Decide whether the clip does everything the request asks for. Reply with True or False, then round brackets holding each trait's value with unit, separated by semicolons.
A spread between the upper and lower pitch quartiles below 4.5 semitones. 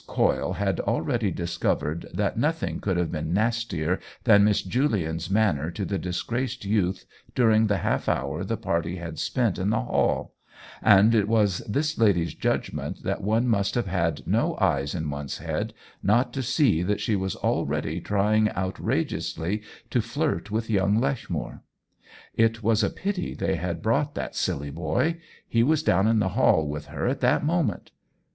False (4.8 semitones)